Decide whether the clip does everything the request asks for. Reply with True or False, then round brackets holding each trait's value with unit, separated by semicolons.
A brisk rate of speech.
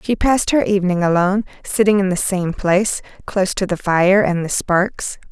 False (190 wpm)